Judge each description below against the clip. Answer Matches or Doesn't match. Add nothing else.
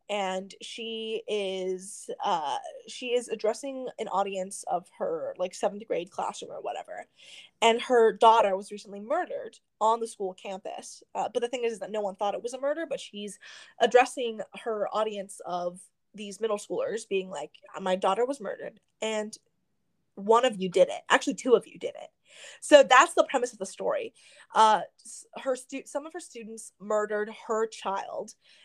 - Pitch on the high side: Matches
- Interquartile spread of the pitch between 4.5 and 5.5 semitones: Matches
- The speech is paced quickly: Doesn't match